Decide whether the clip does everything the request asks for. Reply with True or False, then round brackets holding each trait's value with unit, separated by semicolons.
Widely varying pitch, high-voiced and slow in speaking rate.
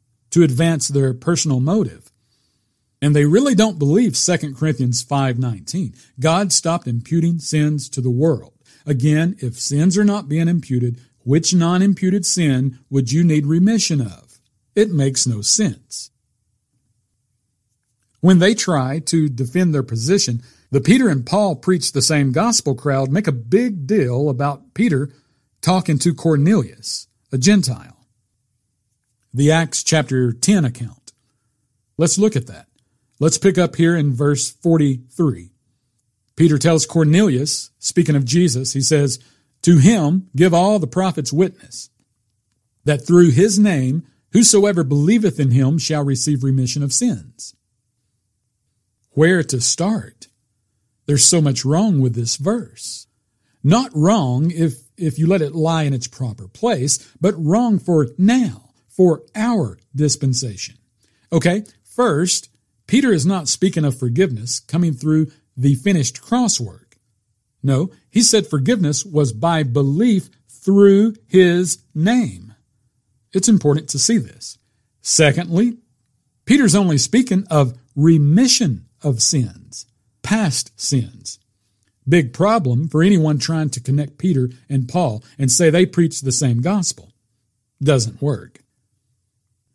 False (6.0 semitones; 140 Hz; 130 wpm)